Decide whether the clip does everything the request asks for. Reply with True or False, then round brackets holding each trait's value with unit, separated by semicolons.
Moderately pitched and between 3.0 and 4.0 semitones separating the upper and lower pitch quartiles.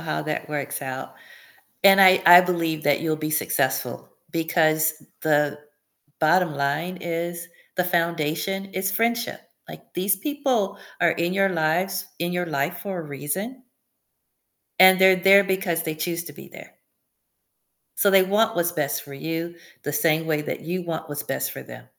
True (170 Hz; 3.3 semitones)